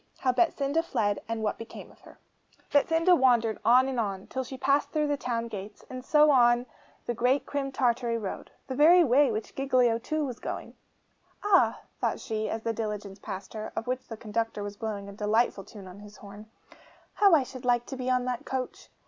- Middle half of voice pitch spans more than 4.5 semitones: No, average, 3.7 semitones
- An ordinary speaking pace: No, fast, 210 wpm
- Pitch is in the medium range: No, high, 240 Hz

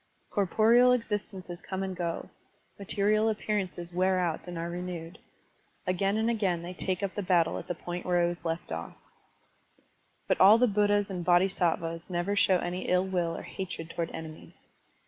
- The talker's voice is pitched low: No, medium, 185 Hz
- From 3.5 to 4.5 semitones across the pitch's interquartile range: No, narrow, 2.6 semitones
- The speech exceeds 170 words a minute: Yes, average, 180 wpm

